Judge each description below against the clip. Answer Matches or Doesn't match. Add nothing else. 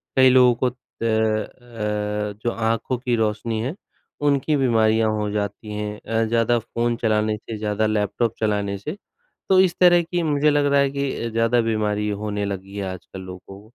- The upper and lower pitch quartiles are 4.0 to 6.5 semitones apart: Doesn't match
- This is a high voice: Doesn't match